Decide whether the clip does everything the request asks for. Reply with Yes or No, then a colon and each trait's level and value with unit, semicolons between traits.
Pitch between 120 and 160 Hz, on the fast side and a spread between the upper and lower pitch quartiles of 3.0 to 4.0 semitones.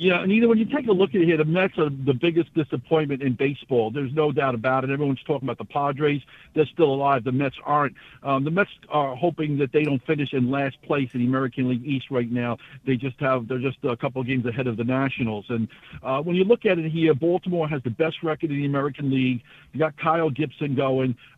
Yes: medium, 140 Hz; fast, 250 wpm; average, 3.3 semitones